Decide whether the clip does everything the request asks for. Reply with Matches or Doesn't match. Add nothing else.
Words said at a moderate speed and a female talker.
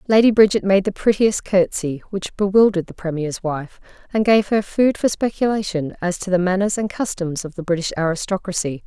Matches